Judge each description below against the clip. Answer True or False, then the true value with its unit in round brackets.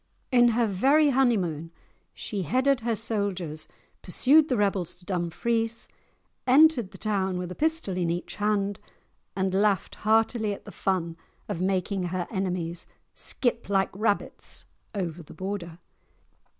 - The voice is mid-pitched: False (200 Hz)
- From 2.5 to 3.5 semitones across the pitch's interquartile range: False (4.3 semitones)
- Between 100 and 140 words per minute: True (135 wpm)